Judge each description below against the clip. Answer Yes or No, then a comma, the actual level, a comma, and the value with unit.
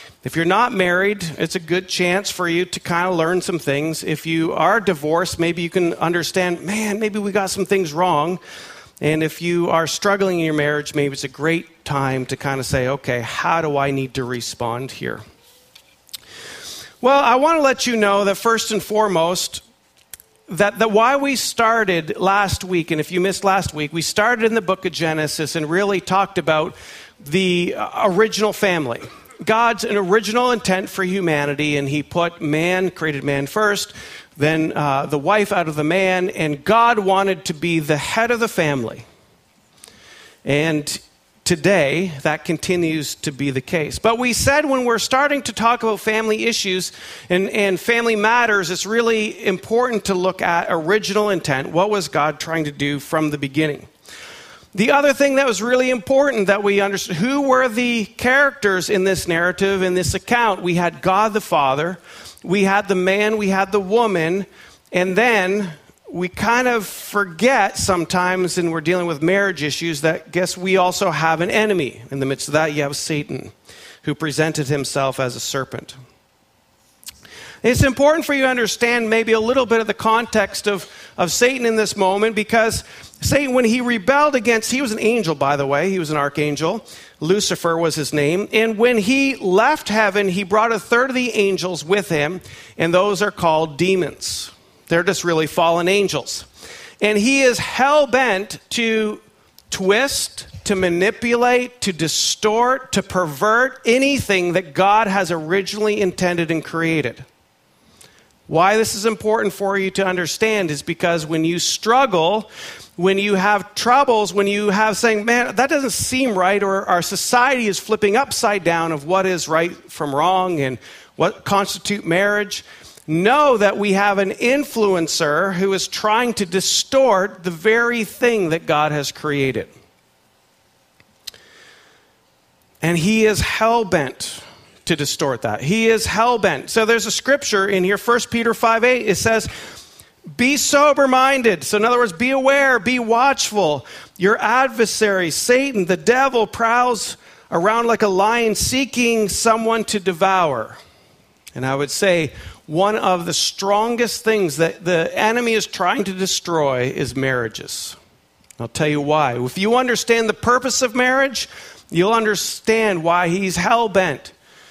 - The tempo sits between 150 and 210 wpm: Yes, average, 165 wpm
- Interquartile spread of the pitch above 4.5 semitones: Yes, average, 5.3 semitones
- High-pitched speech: Yes, high, 195 Hz